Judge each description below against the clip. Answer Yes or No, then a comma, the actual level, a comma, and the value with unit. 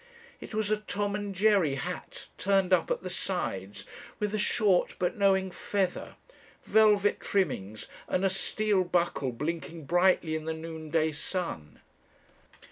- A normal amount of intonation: Yes, average, 4.1 semitones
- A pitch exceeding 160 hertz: Yes, medium, 185 Hz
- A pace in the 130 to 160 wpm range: Yes, average, 140 wpm